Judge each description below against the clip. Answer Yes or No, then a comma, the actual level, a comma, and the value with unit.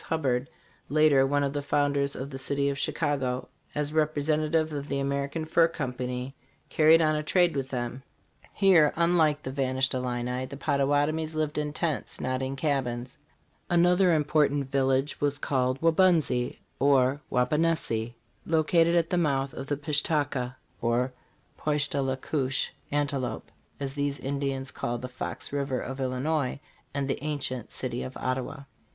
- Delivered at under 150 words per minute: No, average, 160 wpm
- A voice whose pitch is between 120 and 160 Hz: Yes, medium, 140 Hz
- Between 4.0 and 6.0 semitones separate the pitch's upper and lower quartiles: No, average, 2.7 semitones